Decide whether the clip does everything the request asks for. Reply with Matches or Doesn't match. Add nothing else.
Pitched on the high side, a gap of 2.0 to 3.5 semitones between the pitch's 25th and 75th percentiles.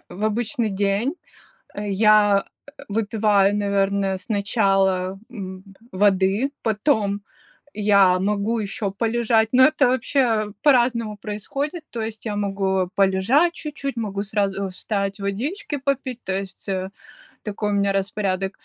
Matches